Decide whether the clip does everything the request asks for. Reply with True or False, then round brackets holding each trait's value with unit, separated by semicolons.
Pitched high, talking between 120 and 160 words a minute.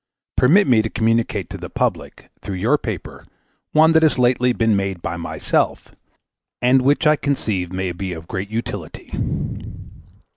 False (115 Hz; 155 wpm)